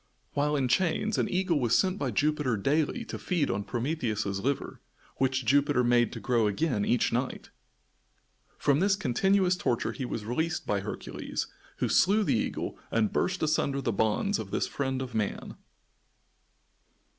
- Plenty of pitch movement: Yes, wide, 5.9 semitones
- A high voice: No, low, 135 Hz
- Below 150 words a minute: No, average, 160 wpm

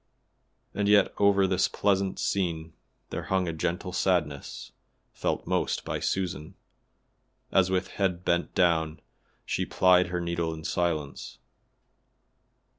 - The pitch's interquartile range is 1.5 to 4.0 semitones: Yes, narrow, 2.4 semitones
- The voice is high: No, very low, 90 Hz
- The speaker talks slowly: Yes, slow, 120 wpm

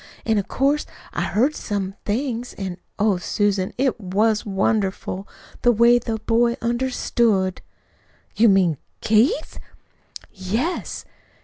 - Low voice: No, high, 220 Hz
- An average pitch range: Yes, average, 3.7 semitones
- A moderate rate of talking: No, slow, 115 wpm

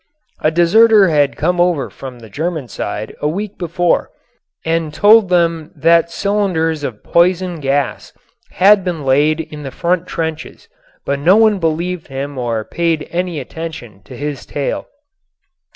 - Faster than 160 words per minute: No, average, 150 wpm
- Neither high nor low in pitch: Yes, medium, 165 Hz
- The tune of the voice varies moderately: Yes, average, 3.7 semitones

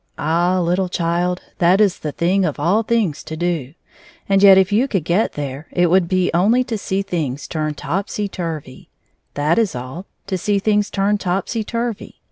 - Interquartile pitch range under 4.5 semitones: Yes, average, 3.6 semitones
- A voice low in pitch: No, medium, 180 Hz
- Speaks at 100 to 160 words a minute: No, average, 180 wpm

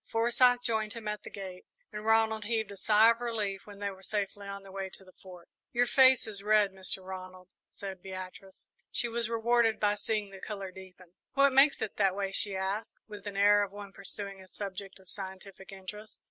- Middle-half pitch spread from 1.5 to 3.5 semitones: Yes, narrow, 2.4 semitones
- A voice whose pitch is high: Yes, high, 200 Hz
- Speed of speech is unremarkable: No, fast, 210 wpm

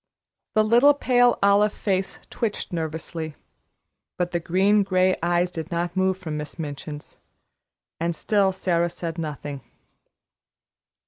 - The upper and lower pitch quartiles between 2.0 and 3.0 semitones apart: No, average, 3.5 semitones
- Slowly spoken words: Yes, slow, 125 wpm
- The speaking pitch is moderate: Yes, medium, 175 Hz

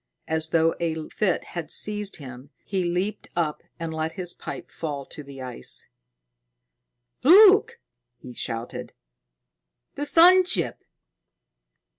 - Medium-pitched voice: Yes, medium, 170 Hz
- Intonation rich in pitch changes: Yes, wide, 6.0 semitones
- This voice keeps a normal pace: No, slow, 120 wpm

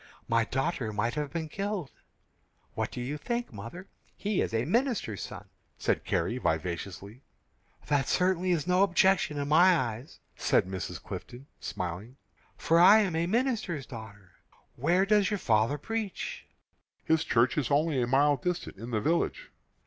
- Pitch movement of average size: No, wide, 7.9 semitones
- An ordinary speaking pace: Yes, average, 155 wpm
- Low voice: No, medium, 150 Hz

